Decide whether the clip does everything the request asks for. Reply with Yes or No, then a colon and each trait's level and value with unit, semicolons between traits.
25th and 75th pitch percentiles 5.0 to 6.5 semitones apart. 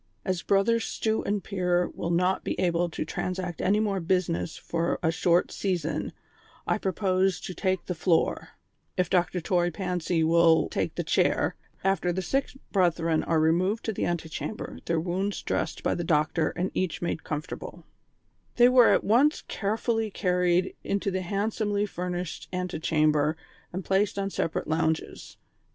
No: average, 2.8 semitones